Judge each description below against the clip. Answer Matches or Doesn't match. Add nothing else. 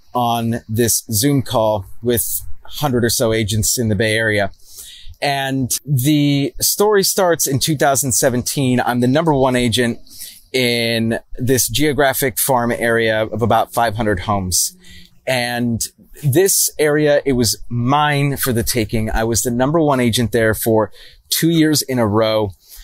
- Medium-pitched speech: Doesn't match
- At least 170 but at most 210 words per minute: Doesn't match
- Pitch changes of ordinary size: Matches